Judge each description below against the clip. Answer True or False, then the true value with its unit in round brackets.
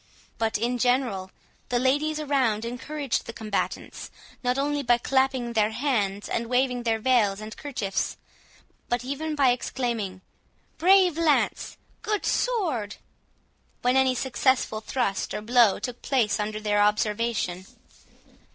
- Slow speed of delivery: True (130 wpm)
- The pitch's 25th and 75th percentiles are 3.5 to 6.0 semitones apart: True (3.9 semitones)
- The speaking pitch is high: True (245 Hz)